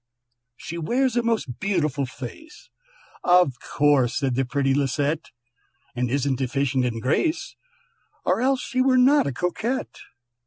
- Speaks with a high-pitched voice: No, medium, 145 Hz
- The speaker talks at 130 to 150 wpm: Yes, average, 140 wpm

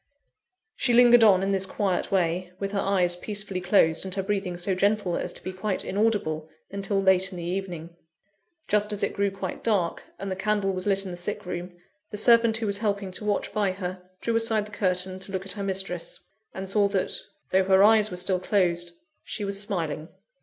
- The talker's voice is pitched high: Yes, high, 195 Hz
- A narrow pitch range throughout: Yes, narrow, 2.1 semitones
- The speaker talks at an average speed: No, fast, 210 wpm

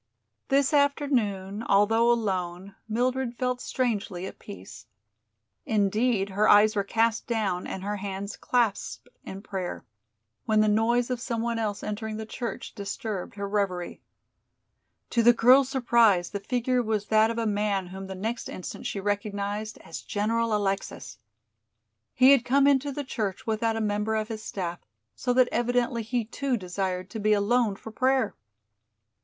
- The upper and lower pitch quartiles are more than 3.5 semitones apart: No, average, 3.1 semitones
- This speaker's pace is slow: No, average, 160 wpm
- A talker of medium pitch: No, high, 215 Hz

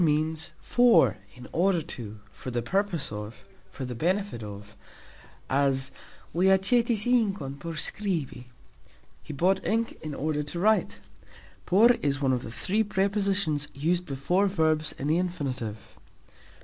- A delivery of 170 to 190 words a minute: No, average, 145 wpm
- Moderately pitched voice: Yes, medium, 160 Hz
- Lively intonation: Yes, wide, 6.4 semitones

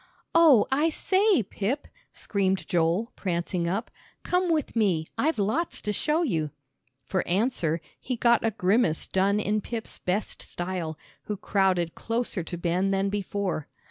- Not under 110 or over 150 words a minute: Yes, average, 145 wpm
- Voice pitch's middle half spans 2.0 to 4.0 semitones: No, average, 4.9 semitones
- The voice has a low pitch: No, high, 200 Hz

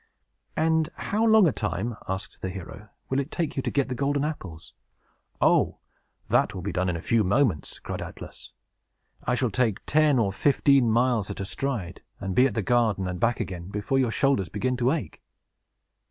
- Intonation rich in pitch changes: Yes, wide, 6.1 semitones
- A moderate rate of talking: Yes, average, 195 wpm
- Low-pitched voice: Yes, low, 120 Hz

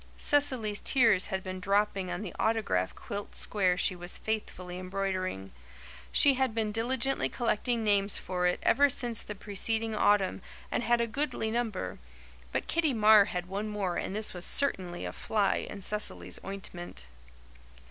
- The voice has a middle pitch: No, high, 205 Hz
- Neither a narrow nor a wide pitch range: Yes, average, 3.5 semitones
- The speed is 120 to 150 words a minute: No, average, 160 wpm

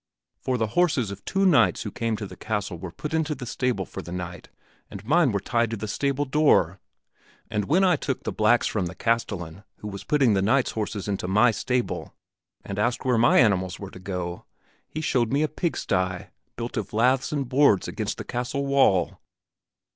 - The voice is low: Yes, low, 115 Hz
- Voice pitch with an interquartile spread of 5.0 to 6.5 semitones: Yes, wide, 5.5 semitones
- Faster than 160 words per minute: Yes, average, 200 wpm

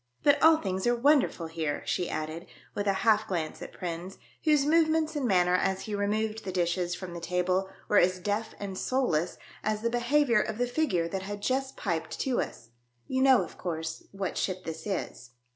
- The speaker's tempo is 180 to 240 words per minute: Yes, average, 200 wpm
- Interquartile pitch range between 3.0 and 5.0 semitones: No, wide, 5.5 semitones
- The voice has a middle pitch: No, high, 200 Hz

